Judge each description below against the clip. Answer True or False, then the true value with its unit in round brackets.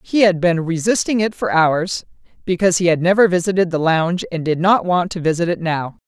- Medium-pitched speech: True (175 Hz)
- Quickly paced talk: True (215 wpm)